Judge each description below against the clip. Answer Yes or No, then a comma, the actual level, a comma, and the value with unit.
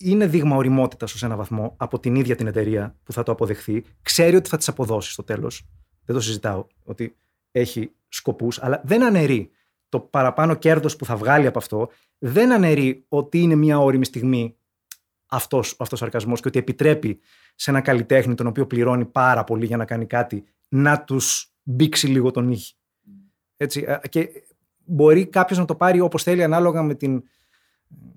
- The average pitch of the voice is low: Yes, low, 130 Hz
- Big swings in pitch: No, average, 4.7 semitones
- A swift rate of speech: Yes, fast, 175 wpm